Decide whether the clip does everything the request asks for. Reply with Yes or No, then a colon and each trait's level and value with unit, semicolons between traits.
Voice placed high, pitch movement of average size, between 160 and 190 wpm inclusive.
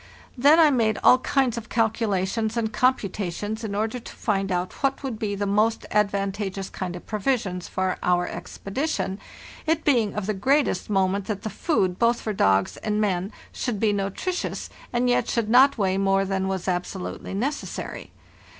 Yes: high, 210 Hz; average, 3.7 semitones; average, 180 wpm